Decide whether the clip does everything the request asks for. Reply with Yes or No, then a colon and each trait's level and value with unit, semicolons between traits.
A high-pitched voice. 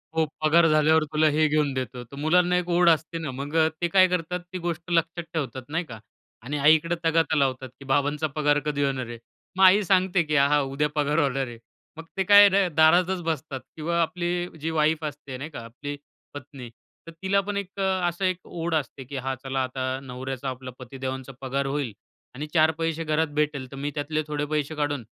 No: medium, 155 Hz